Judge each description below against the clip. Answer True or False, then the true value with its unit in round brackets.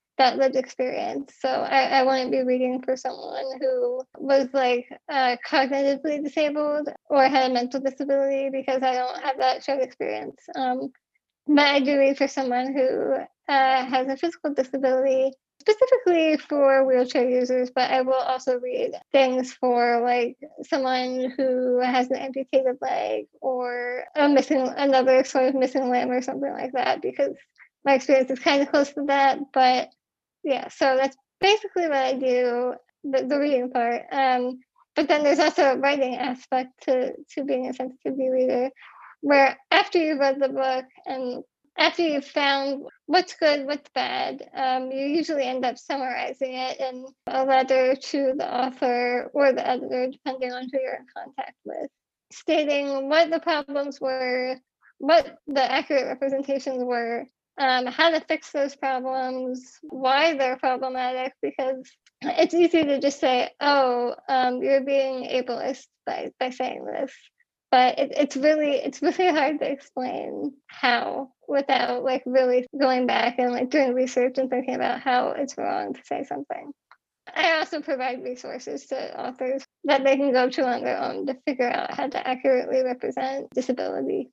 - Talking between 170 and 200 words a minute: False (160 wpm)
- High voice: True (265 Hz)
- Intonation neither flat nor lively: False (2.0 semitones)